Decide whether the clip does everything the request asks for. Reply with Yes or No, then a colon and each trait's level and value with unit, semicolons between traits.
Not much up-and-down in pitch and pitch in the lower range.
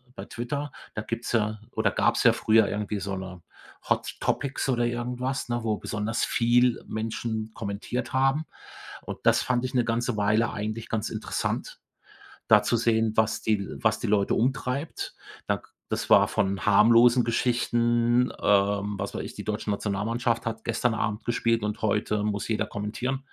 Yes: narrow, 2.3 semitones; low, 115 Hz